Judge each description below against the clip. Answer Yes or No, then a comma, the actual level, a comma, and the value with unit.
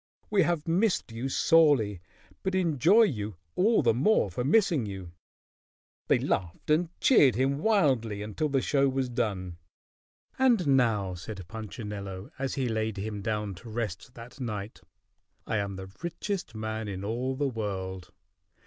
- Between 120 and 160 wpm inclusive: Yes, average, 150 wpm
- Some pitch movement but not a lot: No, wide, 6.2 semitones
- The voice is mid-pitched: No, low, 115 Hz